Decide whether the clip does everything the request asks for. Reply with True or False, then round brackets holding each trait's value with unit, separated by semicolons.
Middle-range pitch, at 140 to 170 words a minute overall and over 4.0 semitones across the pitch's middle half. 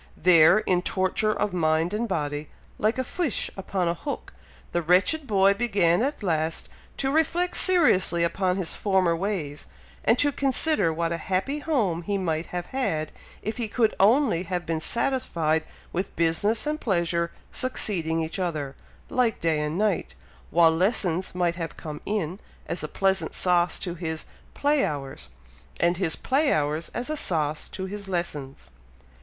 True (180 Hz; 160 wpm; 4.8 semitones)